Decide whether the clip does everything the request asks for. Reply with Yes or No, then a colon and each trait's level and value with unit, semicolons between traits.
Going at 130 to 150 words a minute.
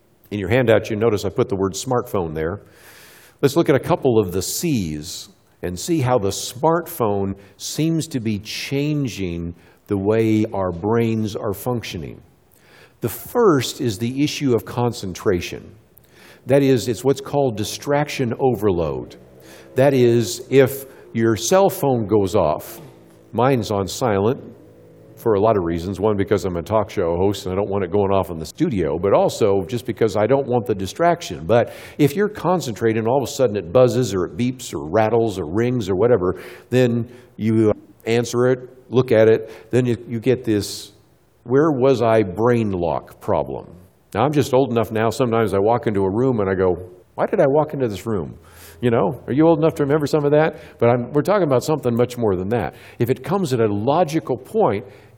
No: average, 190 wpm